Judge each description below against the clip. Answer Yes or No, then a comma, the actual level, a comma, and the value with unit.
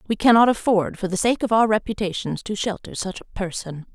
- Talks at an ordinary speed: No, fast, 215 wpm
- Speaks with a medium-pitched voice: No, high, 205 Hz